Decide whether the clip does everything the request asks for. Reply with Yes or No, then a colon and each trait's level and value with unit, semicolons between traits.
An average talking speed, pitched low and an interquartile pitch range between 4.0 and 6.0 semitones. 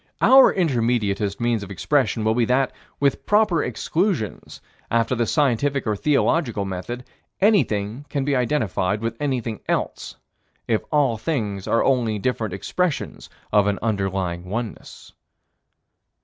No: slow, 130 wpm; low, 115 Hz; average, 5.2 semitones